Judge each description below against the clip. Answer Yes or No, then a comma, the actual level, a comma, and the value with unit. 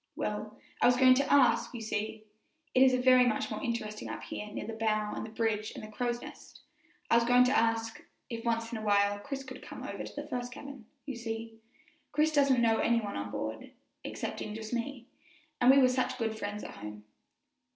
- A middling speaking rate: No, fast, 215 wpm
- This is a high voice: Yes, high, 230 Hz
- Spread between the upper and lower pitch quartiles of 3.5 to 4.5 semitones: No, average, 2.7 semitones